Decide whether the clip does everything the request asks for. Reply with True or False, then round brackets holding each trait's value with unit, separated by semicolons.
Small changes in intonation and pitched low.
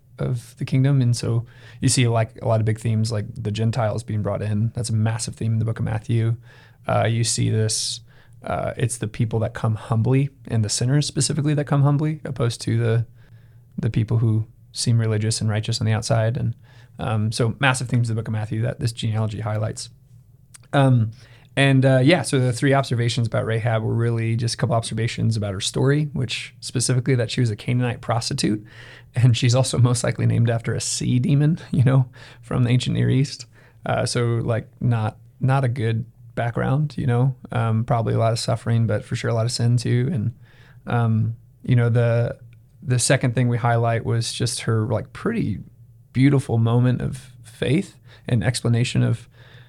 True (1.9 semitones; 120 Hz)